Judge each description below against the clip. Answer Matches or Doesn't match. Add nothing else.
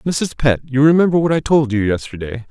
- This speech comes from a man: Matches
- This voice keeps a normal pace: Doesn't match